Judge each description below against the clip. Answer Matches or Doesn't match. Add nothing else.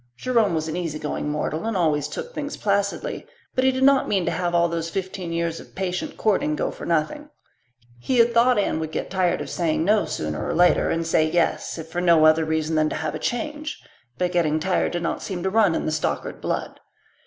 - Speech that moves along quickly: Matches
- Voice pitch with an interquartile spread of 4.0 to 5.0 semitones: Matches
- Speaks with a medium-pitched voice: Matches